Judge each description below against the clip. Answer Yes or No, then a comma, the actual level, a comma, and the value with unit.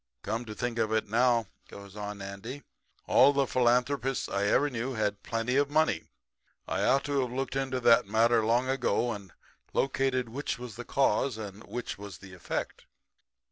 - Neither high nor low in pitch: No, low, 120 Hz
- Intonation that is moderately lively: Yes, average, 3.7 semitones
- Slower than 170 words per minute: No, average, 180 wpm